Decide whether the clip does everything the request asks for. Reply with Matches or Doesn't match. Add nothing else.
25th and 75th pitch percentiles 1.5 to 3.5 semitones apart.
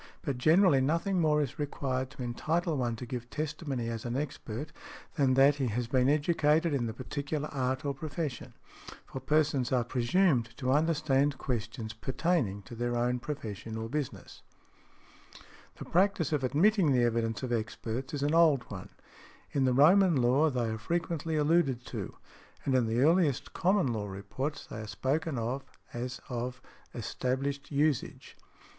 Doesn't match